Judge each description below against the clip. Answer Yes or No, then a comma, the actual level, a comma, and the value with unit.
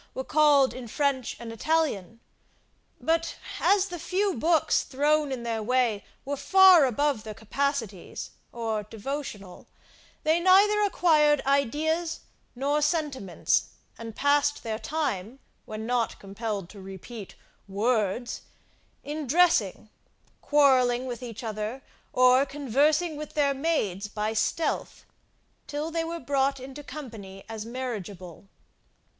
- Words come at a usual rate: No, slow, 120 wpm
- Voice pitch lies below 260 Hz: No, very high, 265 Hz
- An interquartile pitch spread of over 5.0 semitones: Yes, wide, 5.4 semitones